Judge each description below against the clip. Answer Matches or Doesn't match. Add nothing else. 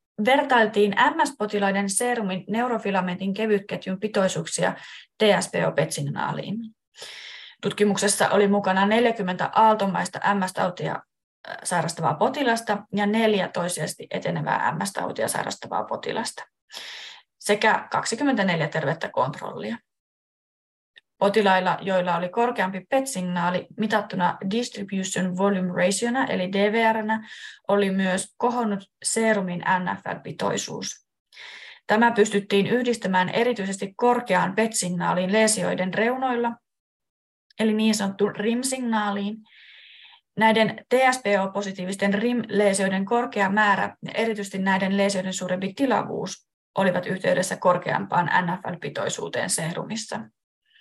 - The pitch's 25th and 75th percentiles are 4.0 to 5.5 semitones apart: Doesn't match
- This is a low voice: Doesn't match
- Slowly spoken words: Matches